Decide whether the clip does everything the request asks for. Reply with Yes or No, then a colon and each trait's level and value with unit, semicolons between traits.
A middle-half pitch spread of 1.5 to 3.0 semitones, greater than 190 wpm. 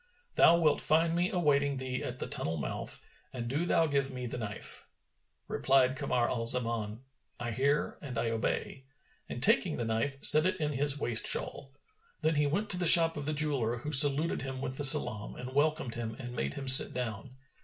No: average, 3.8 semitones; average, 200 wpm